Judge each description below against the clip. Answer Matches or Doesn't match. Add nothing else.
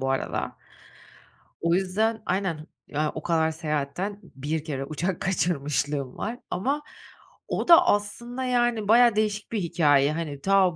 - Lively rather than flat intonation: Matches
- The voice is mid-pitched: Matches